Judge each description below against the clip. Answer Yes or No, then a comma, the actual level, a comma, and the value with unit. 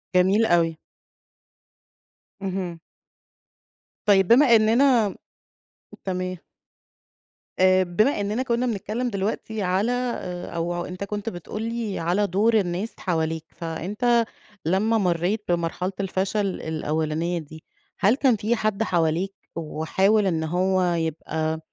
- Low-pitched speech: No, high, 190 Hz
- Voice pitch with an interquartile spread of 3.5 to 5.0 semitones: Yes, average, 3.9 semitones